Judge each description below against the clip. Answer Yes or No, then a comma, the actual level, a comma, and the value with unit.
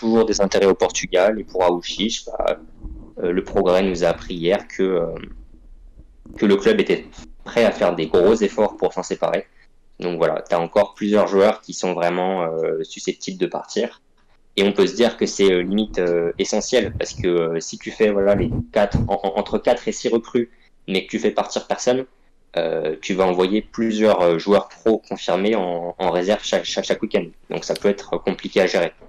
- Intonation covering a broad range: No, average, 3.9 semitones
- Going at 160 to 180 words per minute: No, average, 205 wpm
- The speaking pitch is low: Yes, low, 100 Hz